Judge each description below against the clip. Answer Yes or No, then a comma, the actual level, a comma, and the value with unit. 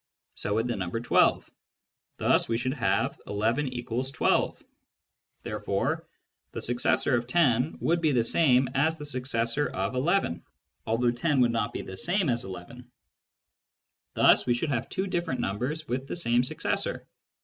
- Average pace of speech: Yes, average, 160 wpm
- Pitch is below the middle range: Yes, low, 125 Hz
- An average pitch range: Yes, average, 4.1 semitones